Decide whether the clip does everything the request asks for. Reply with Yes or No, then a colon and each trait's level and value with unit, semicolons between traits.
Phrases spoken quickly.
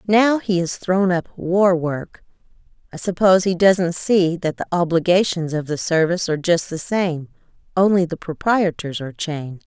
No: average, 165 wpm